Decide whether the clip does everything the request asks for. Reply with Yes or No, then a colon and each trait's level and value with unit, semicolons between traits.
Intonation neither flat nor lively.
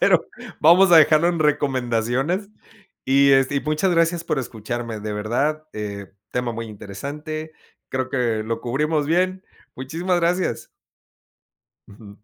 No: wide, 6.0 semitones